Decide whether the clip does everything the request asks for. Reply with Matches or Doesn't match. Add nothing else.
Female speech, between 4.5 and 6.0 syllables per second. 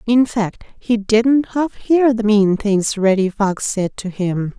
Doesn't match